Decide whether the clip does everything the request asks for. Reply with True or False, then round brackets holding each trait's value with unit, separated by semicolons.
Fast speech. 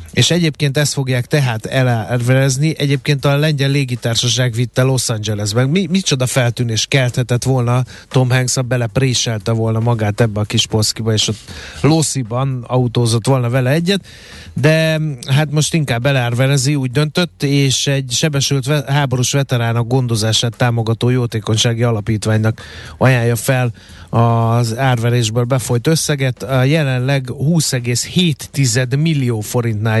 False (120 wpm)